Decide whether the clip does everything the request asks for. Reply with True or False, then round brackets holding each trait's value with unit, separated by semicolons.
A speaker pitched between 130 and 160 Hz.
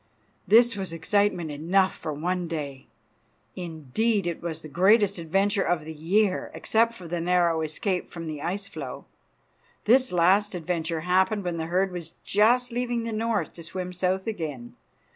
False (180 Hz)